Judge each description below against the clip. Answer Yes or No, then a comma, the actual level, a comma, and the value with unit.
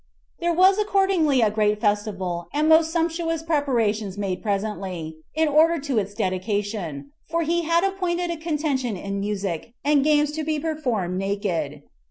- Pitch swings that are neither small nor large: No, wide, 8.3 semitones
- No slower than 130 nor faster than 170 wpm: Yes, average, 155 wpm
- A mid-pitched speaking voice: No, very high, 255 Hz